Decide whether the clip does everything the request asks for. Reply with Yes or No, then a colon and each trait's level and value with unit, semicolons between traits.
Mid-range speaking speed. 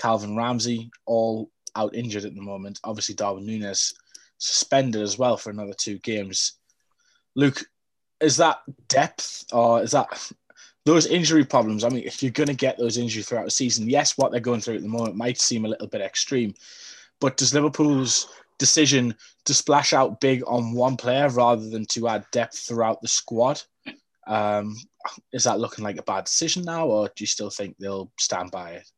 Yes: average, 190 wpm